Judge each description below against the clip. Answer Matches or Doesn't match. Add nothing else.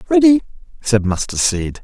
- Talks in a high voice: Doesn't match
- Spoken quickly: Doesn't match